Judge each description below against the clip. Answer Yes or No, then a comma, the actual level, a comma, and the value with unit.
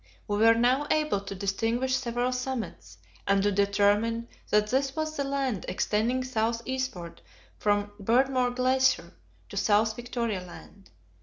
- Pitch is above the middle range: Yes, high, 230 Hz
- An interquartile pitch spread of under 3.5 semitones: No, average, 4.0 semitones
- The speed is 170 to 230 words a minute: No, average, 140 wpm